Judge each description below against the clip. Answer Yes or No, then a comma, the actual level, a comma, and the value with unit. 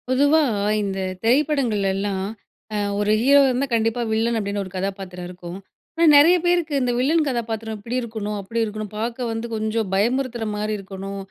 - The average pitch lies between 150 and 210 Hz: No, high, 225 Hz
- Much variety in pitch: No, average, 4.1 semitones